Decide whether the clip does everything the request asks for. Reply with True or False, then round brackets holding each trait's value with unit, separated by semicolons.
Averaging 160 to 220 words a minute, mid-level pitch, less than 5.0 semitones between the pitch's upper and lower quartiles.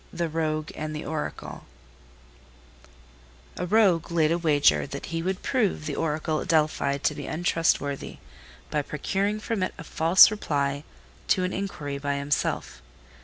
False (150 wpm; 160 Hz; 3.5 semitones)